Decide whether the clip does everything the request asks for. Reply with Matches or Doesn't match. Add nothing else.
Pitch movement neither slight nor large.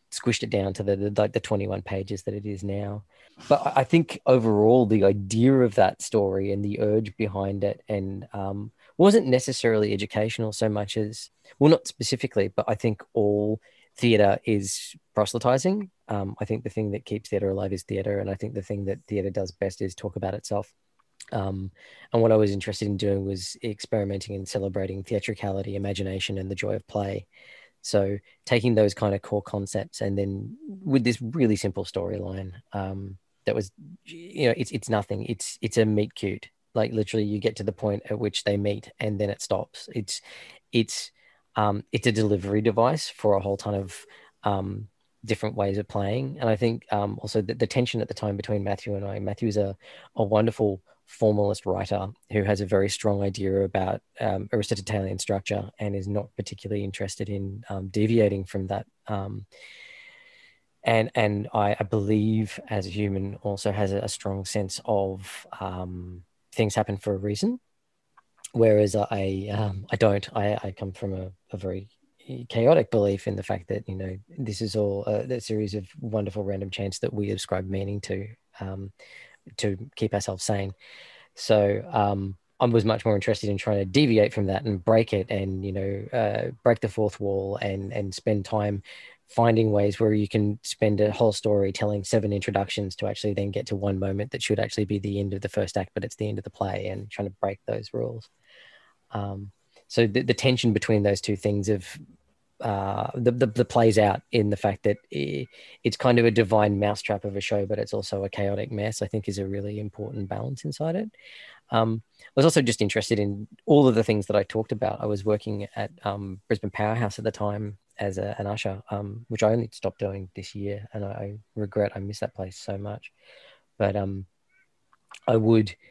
Doesn't match